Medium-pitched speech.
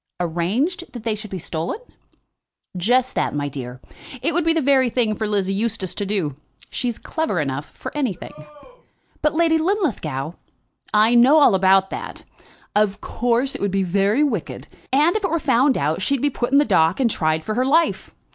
No: high, 220 Hz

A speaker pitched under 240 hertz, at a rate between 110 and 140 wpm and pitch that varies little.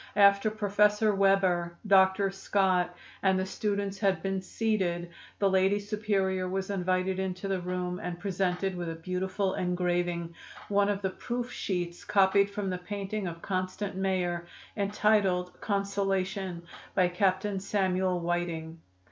Yes: high, 190 Hz; slow, 135 wpm; narrow, 1.8 semitones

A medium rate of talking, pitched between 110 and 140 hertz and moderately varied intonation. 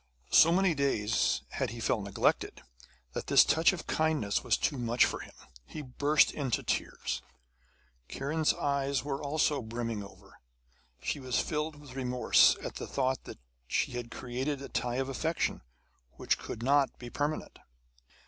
Yes: average, 160 wpm; low, 135 Hz; average, 3.5 semitones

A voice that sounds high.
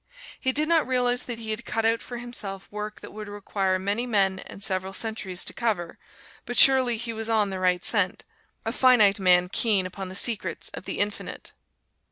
Yes: high, 210 Hz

